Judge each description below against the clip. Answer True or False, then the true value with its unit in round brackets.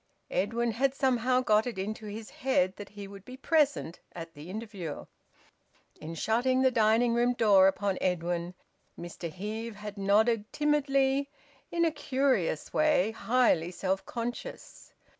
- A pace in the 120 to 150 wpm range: True (140 wpm)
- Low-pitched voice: False (220 Hz)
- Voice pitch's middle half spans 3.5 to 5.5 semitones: True (5.0 semitones)